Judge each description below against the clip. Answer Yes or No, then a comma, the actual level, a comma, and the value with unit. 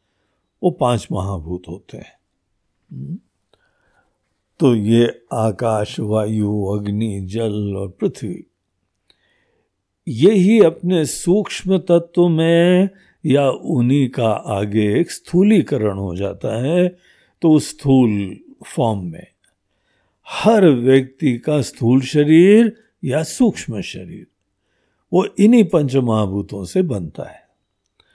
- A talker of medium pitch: No, low, 130 Hz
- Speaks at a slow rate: Yes, slow, 100 wpm